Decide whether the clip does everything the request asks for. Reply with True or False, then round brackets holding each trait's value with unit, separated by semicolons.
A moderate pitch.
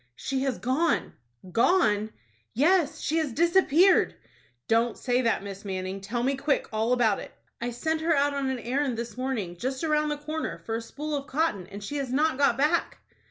False (265 Hz)